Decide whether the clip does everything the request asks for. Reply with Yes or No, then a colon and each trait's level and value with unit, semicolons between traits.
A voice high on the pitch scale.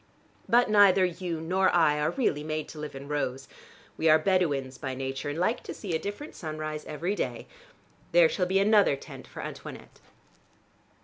No: medium, 160 Hz